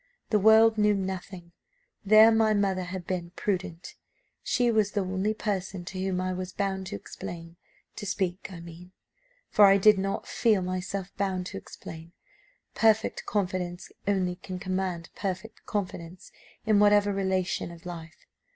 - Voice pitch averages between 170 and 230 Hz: Yes, high, 190 Hz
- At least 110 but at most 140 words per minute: No, average, 150 wpm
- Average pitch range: No, narrow, 2.3 semitones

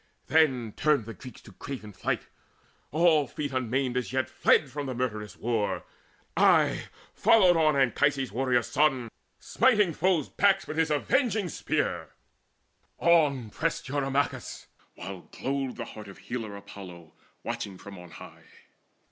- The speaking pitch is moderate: No, low, 130 Hz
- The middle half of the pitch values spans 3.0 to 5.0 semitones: No, wide, 5.4 semitones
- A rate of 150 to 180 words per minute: No, average, 140 wpm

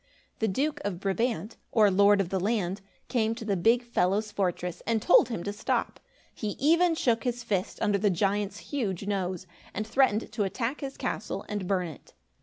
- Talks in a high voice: Yes, high, 205 Hz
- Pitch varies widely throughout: No, average, 3.4 semitones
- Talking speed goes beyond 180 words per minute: Yes, average, 190 wpm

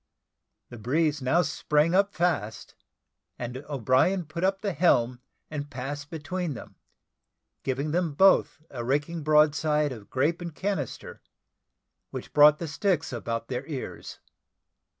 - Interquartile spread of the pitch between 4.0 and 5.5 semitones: Yes, average, 4.4 semitones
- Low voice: No, medium, 150 Hz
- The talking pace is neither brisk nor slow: No, slow, 130 wpm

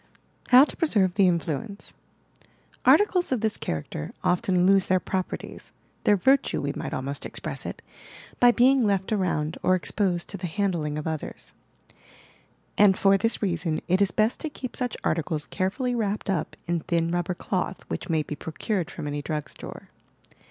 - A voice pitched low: No, medium, 185 Hz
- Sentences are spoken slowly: No, average, 175 wpm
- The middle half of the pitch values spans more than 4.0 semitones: Yes, average, 4.4 semitones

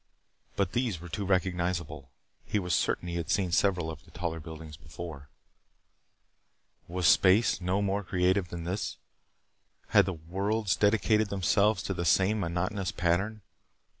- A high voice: No, very low, 90 Hz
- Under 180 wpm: Yes, average, 150 wpm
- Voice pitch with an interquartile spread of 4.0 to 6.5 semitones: No, average, 2.9 semitones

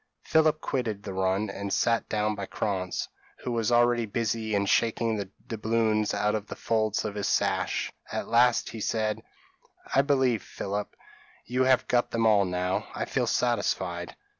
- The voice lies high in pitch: No, low, 110 Hz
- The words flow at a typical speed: Yes, average, 170 wpm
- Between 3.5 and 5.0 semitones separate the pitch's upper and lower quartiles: No, average, 2.7 semitones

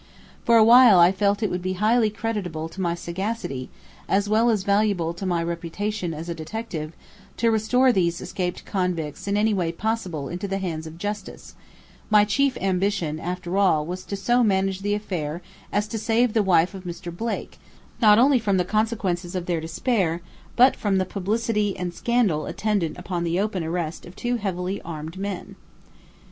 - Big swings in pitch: No, average, 3.7 semitones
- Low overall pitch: No, high, 190 Hz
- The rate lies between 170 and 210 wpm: Yes, average, 180 wpm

